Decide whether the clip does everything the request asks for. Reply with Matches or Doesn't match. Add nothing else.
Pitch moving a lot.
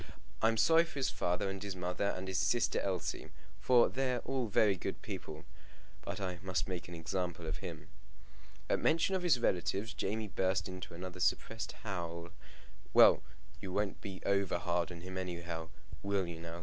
Doesn't match